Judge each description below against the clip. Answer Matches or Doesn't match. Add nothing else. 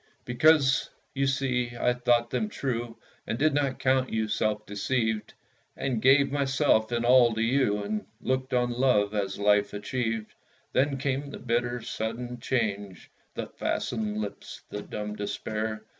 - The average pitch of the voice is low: Matches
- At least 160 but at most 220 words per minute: Doesn't match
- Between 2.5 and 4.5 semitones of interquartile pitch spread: Matches